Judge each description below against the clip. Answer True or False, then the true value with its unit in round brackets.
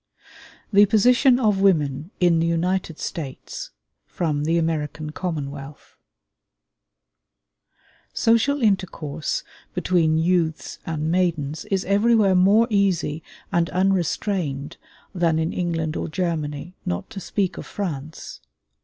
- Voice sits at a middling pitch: True (170 Hz)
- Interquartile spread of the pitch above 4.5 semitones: False (3.8 semitones)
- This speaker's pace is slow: True (110 wpm)